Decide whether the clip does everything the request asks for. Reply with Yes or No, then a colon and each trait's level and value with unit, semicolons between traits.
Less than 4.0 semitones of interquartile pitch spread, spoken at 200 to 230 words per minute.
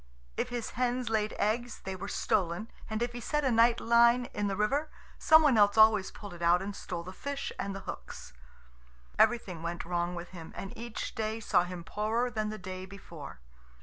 No: average, 4.4 semitones; fast, 205 wpm